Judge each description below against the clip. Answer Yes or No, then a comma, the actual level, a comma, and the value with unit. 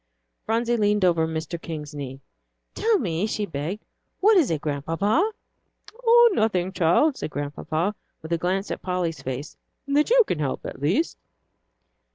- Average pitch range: No, wide, 6.7 semitones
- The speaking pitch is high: No, medium, 180 Hz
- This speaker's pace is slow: No, average, 155 wpm